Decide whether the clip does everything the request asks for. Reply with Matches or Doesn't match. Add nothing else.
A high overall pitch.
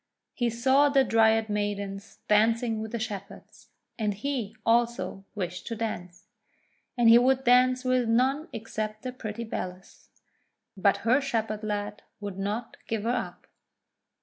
Matches